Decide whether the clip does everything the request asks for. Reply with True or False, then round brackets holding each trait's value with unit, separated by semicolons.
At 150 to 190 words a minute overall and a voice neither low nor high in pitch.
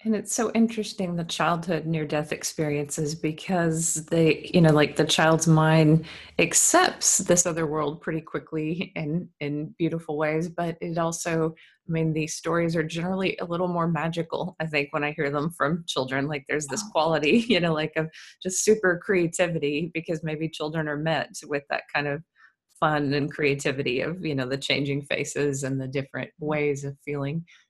True (180 wpm; 160 Hz)